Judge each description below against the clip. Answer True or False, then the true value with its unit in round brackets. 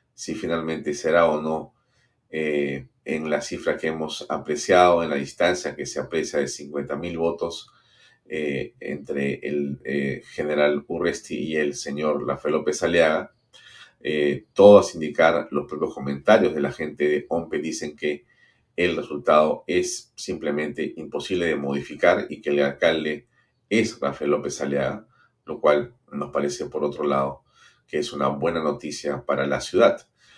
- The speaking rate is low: False (150 wpm)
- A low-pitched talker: True (75 Hz)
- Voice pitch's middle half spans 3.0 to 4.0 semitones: False (2.4 semitones)